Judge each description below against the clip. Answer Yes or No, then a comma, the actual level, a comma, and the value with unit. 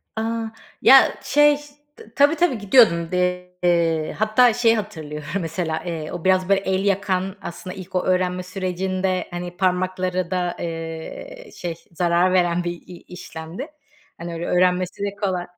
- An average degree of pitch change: No, narrow, 2.3 semitones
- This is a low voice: No, medium, 185 Hz